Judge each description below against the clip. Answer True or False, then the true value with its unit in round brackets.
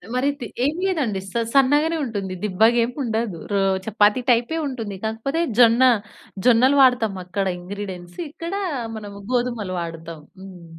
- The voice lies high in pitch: True (225 Hz)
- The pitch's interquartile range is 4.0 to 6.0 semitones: True (4.6 semitones)